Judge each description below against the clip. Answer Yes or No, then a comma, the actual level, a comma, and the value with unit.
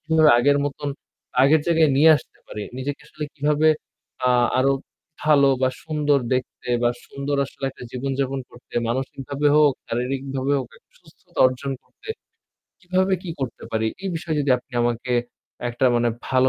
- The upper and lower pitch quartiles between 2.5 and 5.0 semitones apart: Yes, average, 2.8 semitones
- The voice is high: No, medium, 140 Hz